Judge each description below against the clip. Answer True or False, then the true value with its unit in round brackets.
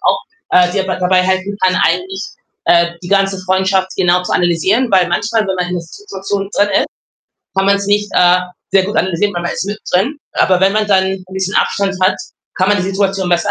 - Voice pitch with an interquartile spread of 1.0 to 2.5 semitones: True (1.7 semitones)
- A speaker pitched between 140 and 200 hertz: True (190 Hz)